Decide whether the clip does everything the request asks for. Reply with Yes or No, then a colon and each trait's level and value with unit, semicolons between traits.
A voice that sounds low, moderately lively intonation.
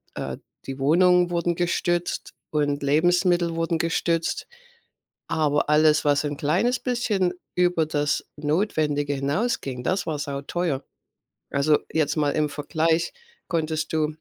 No: medium, 155 Hz; average, 3.1 semitones